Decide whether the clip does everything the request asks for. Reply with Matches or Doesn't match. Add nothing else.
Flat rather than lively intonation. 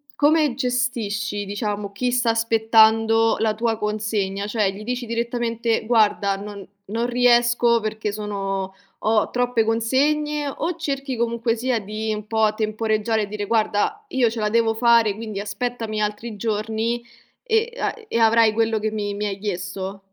Matches